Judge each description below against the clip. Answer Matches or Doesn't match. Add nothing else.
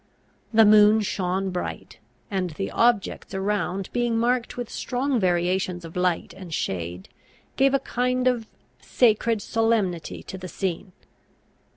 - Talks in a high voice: Matches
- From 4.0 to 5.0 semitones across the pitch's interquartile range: Matches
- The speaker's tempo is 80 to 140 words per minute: Matches